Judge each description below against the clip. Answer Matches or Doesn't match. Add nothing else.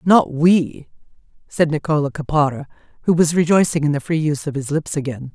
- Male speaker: Doesn't match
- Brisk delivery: Doesn't match